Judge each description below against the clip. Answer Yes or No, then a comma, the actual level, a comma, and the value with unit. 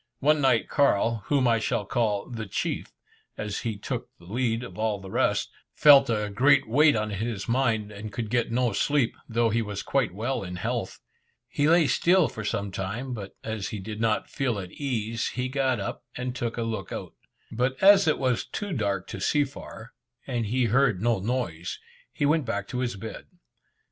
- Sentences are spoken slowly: No, average, 200 wpm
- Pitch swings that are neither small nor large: Yes, average, 3.7 semitones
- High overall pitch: No, low, 115 Hz